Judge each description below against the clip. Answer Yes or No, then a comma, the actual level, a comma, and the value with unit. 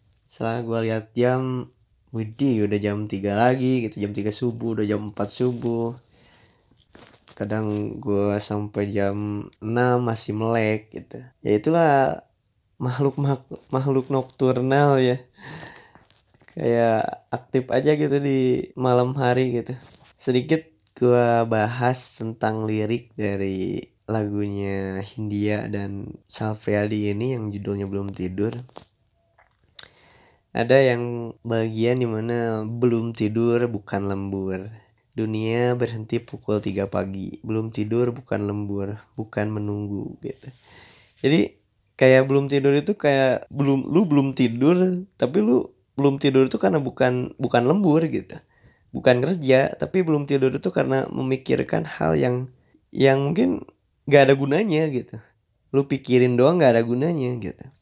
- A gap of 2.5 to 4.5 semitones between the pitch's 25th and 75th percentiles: Yes, average, 3.8 semitones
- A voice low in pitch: Yes, low, 120 Hz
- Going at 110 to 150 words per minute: Yes, average, 120 wpm